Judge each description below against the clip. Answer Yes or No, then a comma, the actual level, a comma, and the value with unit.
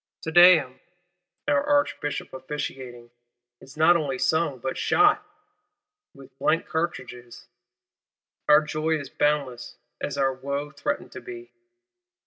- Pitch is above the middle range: No, medium, 150 Hz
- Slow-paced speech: Yes, slow, 110 wpm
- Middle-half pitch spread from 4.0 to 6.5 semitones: Yes, average, 4.7 semitones